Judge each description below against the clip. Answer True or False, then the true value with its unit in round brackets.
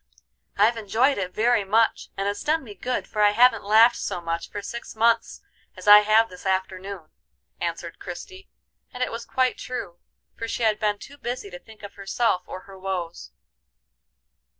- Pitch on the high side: True (210 Hz)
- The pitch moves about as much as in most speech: True (3.4 semitones)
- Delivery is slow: False (180 wpm)